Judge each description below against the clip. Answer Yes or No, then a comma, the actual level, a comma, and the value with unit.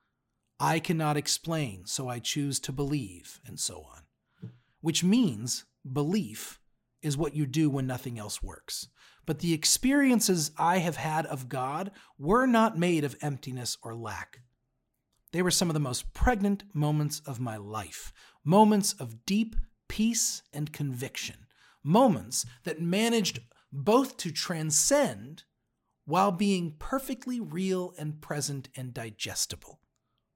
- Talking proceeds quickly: No, slow, 135 wpm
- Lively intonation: Yes, wide, 6.6 semitones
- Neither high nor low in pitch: Yes, medium, 150 Hz